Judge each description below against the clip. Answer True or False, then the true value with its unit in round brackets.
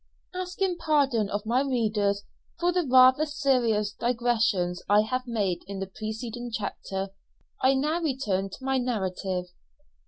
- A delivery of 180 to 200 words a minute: False (135 wpm)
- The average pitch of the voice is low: False (235 Hz)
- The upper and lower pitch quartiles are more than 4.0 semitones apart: True (4.7 semitones)